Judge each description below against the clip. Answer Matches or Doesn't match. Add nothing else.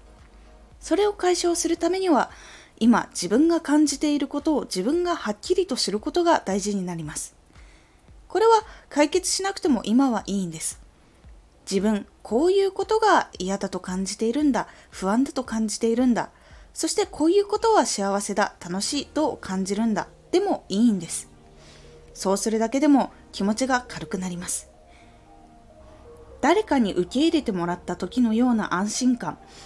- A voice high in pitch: Matches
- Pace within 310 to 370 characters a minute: Matches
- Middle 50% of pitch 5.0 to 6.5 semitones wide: Doesn't match